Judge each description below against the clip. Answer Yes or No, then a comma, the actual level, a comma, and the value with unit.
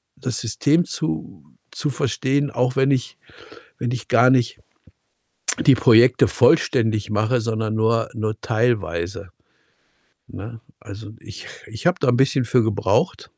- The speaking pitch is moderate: No, low, 115 Hz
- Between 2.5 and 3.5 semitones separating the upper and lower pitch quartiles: Yes, average, 2.9 semitones